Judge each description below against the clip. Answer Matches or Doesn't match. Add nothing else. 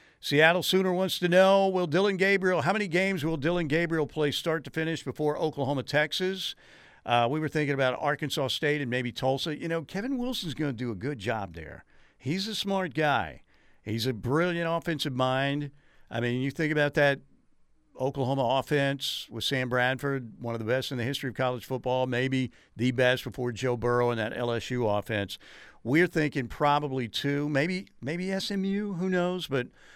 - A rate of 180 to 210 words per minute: Matches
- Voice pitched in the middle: Matches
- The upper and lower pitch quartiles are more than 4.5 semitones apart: Matches